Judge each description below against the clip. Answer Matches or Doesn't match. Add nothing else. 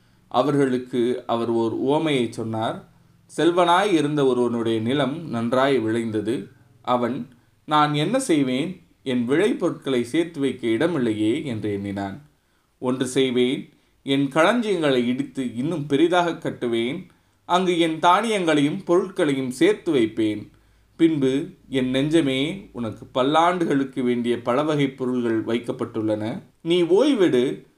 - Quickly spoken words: Doesn't match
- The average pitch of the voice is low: Matches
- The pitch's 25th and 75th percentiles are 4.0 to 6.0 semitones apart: Matches